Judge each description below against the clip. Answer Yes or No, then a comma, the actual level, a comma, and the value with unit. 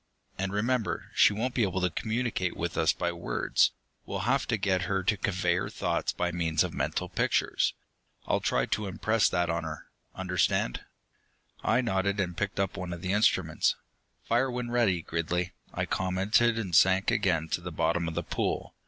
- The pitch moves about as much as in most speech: Yes, average, 3.4 semitones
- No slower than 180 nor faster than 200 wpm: Yes, average, 185 wpm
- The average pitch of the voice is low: Yes, very low, 95 Hz